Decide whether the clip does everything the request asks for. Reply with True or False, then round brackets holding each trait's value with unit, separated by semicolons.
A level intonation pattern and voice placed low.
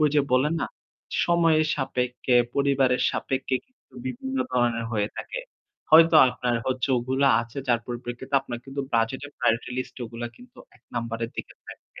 False (3.0 semitones; 130 Hz)